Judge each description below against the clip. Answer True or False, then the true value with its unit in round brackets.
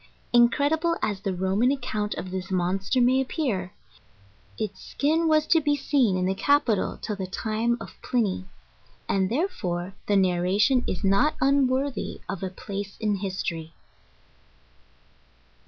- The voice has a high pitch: True (210 Hz)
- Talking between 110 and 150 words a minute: True (140 wpm)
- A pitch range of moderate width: False (5.9 semitones)